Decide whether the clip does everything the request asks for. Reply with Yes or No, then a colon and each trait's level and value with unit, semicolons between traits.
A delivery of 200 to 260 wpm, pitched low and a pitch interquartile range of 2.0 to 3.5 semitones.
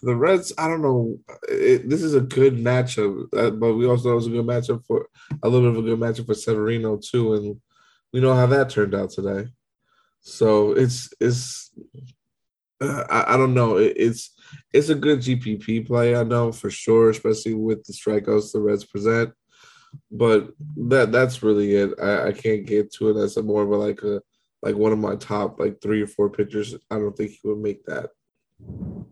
Yes: fast, 205 wpm; low, 115 Hz; average, 3.1 semitones